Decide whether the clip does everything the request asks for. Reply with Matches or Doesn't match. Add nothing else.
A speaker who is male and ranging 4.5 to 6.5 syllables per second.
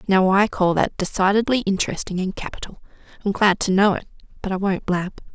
Doesn't match